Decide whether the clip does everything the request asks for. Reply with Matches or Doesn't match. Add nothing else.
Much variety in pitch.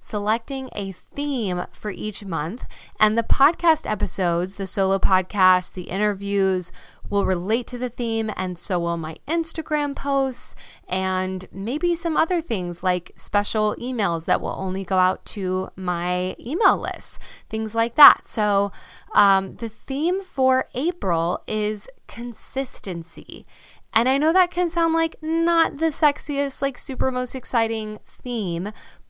Matches